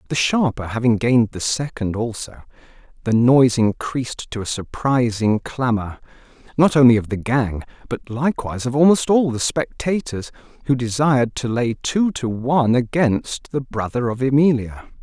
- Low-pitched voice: Yes, low, 125 Hz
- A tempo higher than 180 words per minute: No, average, 150 wpm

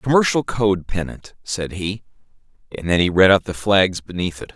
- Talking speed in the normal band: Yes, average, 185 wpm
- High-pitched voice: No, low, 100 Hz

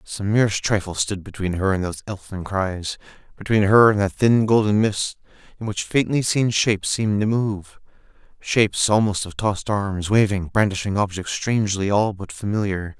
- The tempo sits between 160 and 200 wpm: Yes, average, 165 wpm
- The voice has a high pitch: No, low, 100 Hz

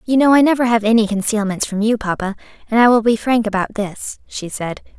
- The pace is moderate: No, fast, 230 wpm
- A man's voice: No, female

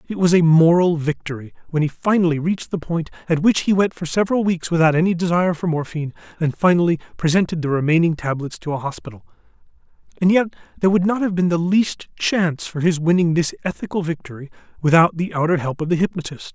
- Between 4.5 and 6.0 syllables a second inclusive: No, 6.5 syllables/s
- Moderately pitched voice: Yes, medium, 170 Hz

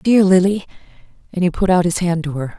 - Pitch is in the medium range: Yes, medium, 180 Hz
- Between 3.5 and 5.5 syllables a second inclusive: Yes, 5.3 syllables/s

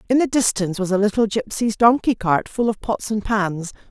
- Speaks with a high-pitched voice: Yes, high, 210 Hz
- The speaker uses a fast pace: Yes, fast, 215 wpm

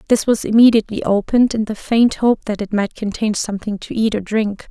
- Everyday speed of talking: No, fast, 215 wpm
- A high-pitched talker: Yes, high, 215 Hz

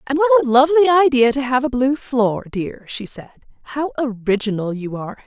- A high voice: Yes, very high, 255 Hz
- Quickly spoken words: No, average, 195 wpm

